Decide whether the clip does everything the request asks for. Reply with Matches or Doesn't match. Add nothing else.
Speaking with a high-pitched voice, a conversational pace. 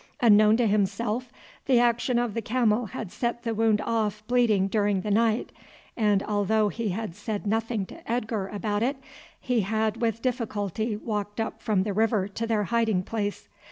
Matches